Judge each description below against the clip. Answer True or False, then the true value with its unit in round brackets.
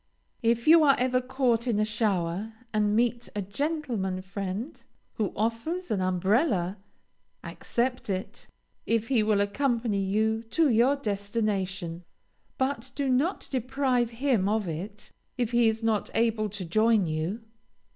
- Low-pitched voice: False (225 Hz)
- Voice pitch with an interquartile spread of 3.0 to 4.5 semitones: True (3.8 semitones)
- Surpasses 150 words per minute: False (140 wpm)